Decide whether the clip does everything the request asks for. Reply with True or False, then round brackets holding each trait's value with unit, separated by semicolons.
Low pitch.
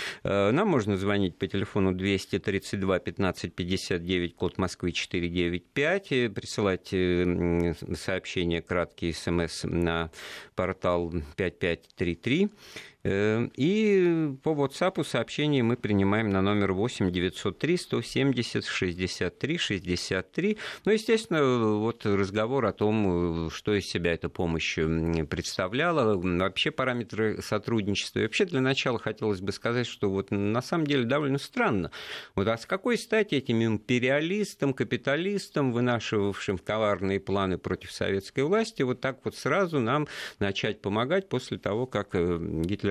True (105 Hz)